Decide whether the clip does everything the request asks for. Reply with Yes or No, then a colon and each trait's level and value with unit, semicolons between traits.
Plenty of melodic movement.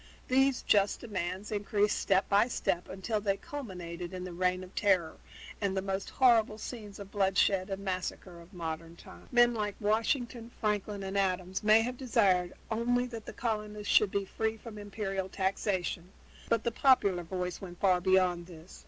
No: average, 3.1 semitones